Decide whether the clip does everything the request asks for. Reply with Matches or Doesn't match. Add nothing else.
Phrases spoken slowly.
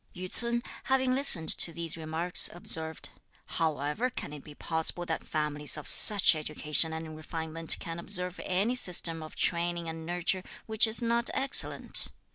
Doesn't match